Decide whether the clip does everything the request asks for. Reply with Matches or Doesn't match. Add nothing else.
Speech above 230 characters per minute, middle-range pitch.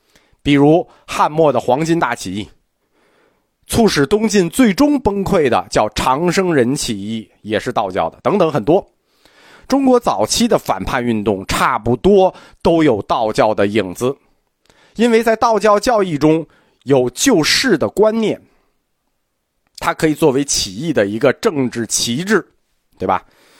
Doesn't match